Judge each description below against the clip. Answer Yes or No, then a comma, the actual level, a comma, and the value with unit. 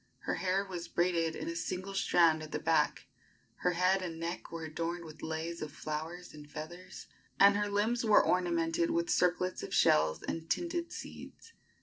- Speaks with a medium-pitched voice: Yes, medium, 170 Hz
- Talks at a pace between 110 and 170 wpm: No, average, 180 wpm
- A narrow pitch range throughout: Yes, narrow, 2.3 semitones